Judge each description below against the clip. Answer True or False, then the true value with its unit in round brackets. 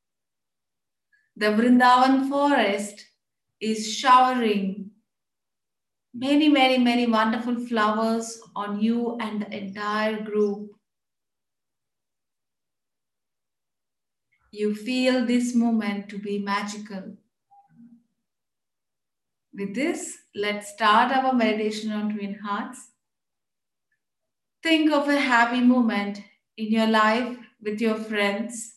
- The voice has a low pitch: False (220 Hz)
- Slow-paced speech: True (90 wpm)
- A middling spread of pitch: True (3.0 semitones)